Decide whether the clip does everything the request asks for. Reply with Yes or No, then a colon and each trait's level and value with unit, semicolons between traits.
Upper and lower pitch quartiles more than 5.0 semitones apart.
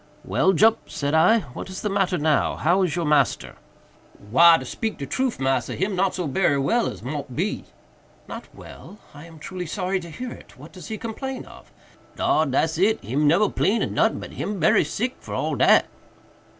Yes: wide, 5.4 semitones